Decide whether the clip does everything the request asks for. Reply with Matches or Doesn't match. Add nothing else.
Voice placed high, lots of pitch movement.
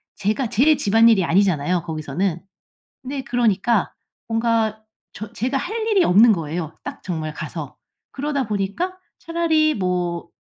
Matches